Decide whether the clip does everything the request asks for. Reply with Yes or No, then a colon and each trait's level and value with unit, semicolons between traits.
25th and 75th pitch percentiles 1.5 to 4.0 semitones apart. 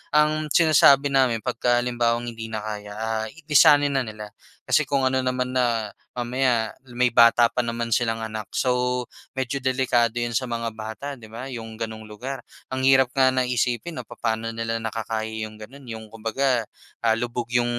Yes: narrow, 2.6 semitones